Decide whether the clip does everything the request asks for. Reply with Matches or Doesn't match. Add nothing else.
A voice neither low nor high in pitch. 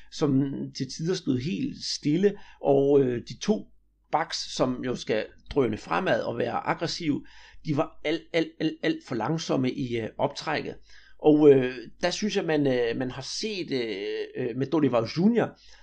Matches